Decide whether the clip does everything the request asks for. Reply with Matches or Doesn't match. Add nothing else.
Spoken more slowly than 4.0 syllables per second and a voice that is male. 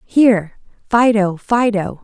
Doesn't match